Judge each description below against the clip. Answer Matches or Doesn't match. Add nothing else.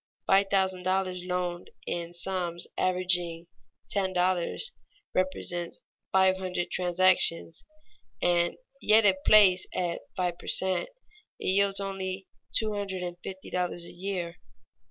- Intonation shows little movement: Matches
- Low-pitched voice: Doesn't match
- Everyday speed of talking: Doesn't match